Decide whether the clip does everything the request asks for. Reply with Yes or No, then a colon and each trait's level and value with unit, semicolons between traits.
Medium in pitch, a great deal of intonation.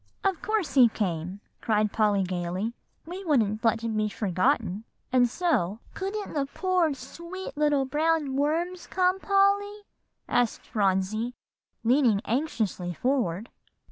No: very high, 250 Hz; wide, 8.2 semitones